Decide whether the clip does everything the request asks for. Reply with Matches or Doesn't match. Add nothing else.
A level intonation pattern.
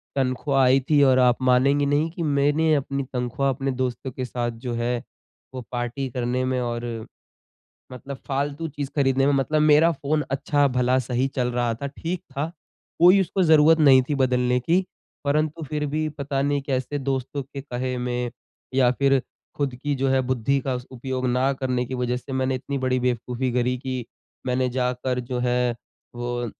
Matches